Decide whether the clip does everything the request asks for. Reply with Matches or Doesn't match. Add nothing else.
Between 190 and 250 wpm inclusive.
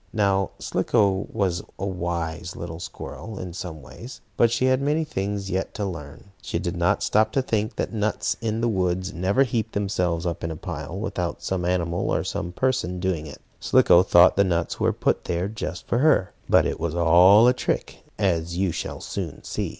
Matches